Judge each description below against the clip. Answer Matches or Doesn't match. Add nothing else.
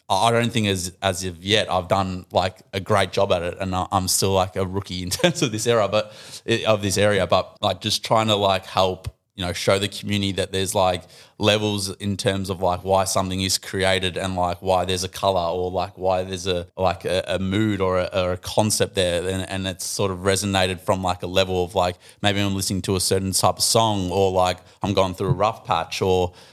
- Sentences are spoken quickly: Matches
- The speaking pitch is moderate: Doesn't match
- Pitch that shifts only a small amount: Matches